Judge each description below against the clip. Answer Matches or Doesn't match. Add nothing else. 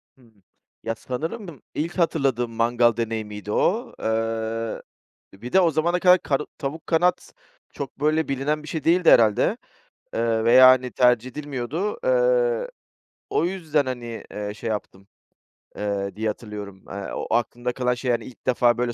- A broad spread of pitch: Matches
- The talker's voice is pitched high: Doesn't match